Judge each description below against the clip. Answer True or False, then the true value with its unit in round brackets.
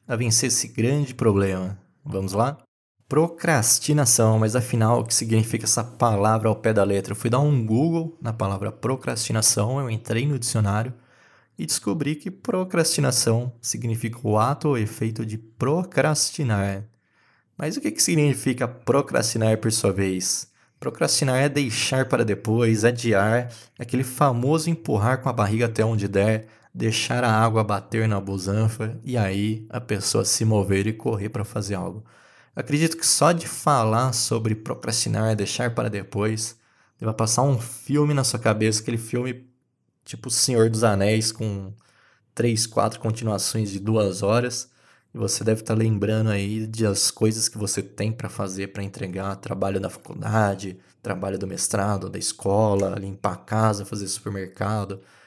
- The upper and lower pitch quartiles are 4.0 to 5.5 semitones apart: False (3.1 semitones)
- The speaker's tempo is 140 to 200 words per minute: True (155 wpm)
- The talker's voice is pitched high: False (110 Hz)